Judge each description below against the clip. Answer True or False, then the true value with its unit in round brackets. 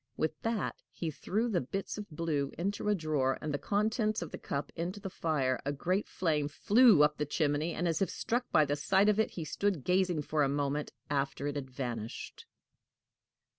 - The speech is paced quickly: True (210 wpm)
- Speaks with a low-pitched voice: False (155 Hz)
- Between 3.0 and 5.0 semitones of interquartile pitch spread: False (5.4 semitones)